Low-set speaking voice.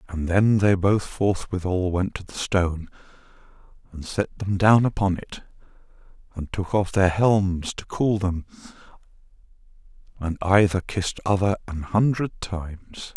Yes: very low, 95 Hz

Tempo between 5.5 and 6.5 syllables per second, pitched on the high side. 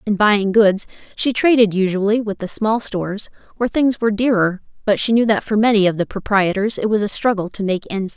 Yes: 5.8 syllables/s; high, 210 Hz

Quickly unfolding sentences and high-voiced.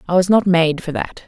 No: fast, 280 wpm; medium, 175 Hz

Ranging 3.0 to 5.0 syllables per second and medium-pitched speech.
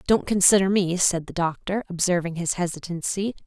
No: 5.4 syllables/s; medium, 180 Hz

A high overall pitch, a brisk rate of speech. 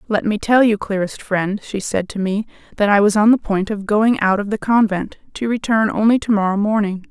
Yes: high, 210 Hz; fast, 230 wpm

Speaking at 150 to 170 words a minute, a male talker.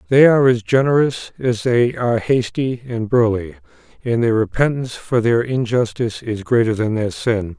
Yes: average, 165 wpm; male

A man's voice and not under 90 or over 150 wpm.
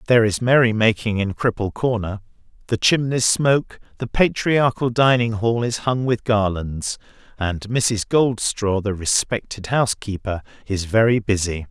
Yes: male; average, 140 wpm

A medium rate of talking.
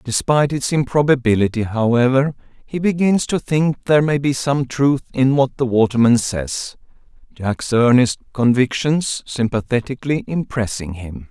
No: slow, 120 wpm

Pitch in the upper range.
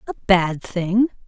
Yes: high, 200 Hz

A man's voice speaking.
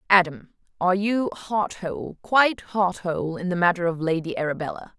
No: female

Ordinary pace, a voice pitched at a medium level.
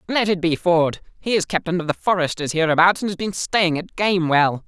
No: fast, 220 wpm; medium, 175 Hz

